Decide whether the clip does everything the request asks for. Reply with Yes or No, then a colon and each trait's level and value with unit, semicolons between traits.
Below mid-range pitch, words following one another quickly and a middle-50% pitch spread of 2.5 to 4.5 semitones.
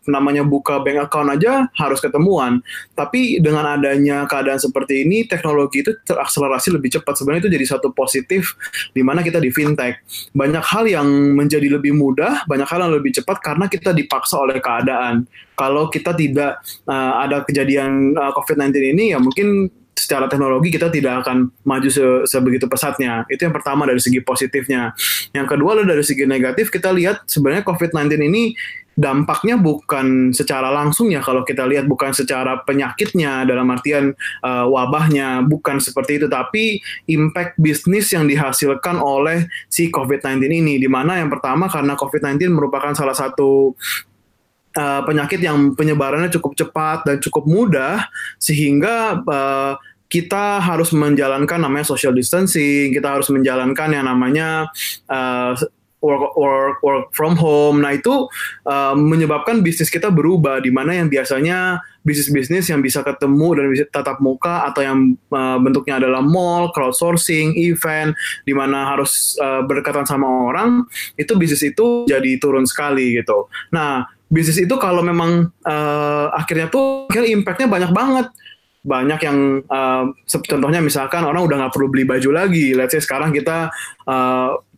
No: medium, 145 Hz; fast, 150 wpm; average, 3.7 semitones